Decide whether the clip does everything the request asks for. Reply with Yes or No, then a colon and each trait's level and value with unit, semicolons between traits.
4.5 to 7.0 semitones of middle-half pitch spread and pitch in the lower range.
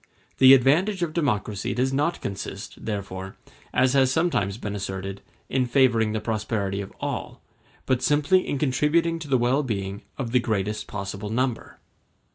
Yes: average, 5.2 semitones; low, 120 Hz